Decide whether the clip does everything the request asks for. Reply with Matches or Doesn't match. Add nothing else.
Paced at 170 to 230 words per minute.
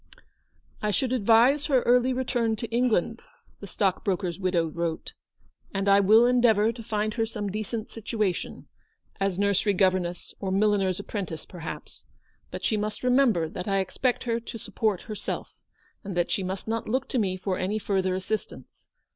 Matches